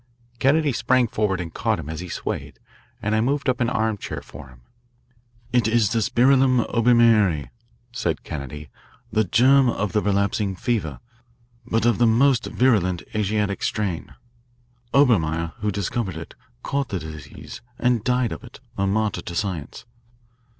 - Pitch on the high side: No, low, 110 Hz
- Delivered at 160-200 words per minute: No, average, 150 wpm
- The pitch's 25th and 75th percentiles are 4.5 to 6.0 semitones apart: Yes, average, 5.2 semitones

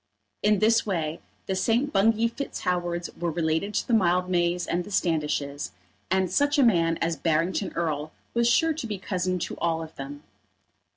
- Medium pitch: Yes, medium, 180 Hz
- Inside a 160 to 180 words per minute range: Yes, average, 170 wpm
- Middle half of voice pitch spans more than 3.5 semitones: Yes, average, 4.4 semitones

